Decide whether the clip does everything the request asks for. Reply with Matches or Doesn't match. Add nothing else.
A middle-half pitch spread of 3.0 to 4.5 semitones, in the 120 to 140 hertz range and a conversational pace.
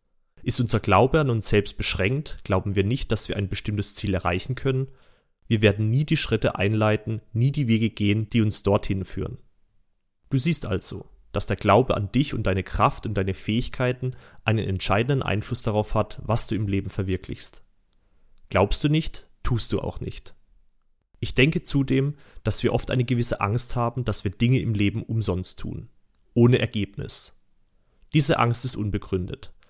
Doesn't match